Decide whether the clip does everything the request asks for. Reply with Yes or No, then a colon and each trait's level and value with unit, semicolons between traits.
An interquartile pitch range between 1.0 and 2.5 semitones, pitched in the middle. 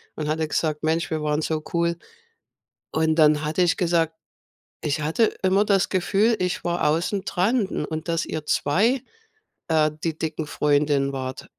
No: average, 2.9 semitones; medium, 160 Hz